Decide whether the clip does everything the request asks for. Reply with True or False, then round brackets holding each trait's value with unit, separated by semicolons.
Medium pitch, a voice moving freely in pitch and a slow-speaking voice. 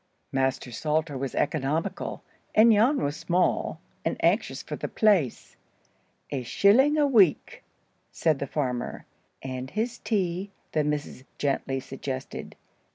True (150 Hz; 7.1 semitones; 125 wpm)